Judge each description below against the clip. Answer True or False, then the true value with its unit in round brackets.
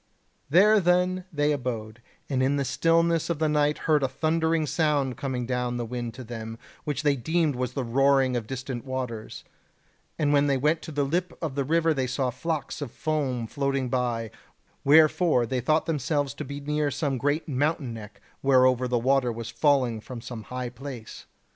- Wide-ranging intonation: False (3.4 semitones)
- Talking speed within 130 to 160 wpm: False (185 wpm)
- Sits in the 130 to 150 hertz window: True (135 Hz)